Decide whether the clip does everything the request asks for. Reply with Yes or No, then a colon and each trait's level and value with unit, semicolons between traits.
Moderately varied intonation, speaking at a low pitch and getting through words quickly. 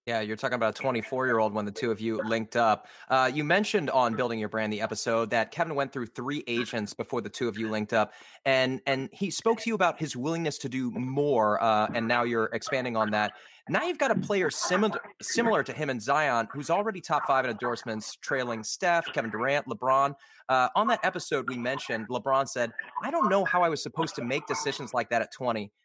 Yes: average, 4.0 semitones; low, 125 Hz; fast, 230 wpm